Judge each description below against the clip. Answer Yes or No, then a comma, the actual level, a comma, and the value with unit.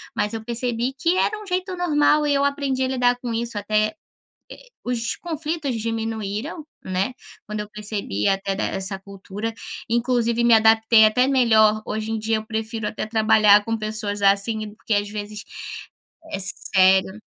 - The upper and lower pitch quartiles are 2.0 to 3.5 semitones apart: Yes, average, 2.9 semitones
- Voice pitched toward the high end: Yes, high, 220 Hz